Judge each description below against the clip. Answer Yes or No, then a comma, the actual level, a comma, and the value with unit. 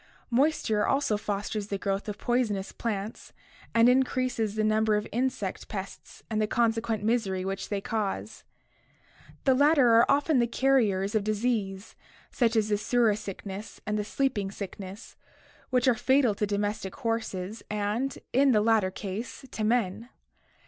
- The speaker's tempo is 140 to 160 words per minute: Yes, average, 150 wpm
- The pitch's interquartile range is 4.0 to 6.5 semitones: No, average, 3.1 semitones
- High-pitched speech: Yes, high, 215 Hz